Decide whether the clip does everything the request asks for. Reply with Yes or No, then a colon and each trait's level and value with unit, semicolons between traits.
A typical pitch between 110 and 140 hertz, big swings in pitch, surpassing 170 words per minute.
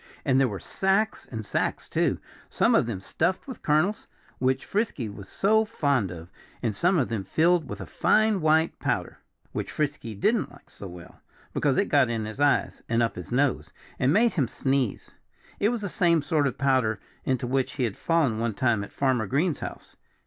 Yes: low, 135 Hz; wide, 6.8 semitones; average, 200 wpm